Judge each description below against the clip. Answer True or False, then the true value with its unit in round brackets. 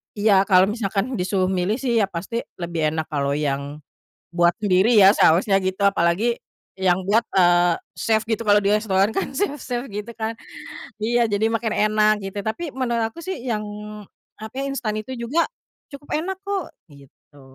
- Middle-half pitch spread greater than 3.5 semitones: True (4.2 semitones)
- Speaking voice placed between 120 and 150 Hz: False (210 Hz)